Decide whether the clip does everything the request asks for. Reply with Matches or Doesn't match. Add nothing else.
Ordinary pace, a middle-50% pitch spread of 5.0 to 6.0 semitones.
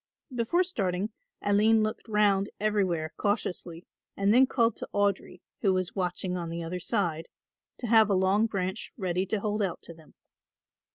Doesn't match